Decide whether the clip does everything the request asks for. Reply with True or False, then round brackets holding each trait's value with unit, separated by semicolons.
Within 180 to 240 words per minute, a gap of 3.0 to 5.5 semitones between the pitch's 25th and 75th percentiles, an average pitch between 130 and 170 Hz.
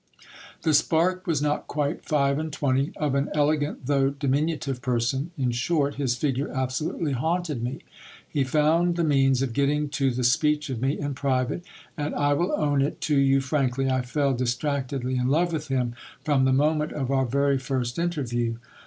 False (190 wpm; 2.5 semitones; 140 Hz)